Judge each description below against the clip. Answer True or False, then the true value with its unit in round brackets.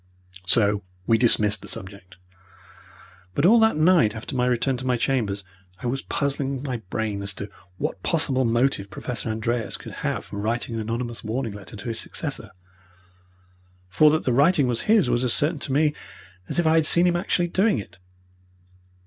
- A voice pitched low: True (120 Hz)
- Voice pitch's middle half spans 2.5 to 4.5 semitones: False (5.1 semitones)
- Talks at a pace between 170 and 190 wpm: True (185 wpm)